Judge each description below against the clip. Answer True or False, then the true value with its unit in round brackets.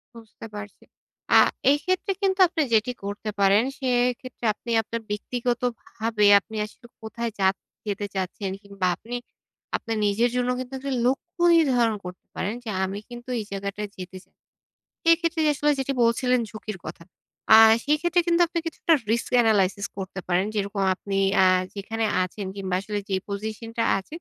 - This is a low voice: False (225 Hz)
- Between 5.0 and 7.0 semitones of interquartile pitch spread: False (3.9 semitones)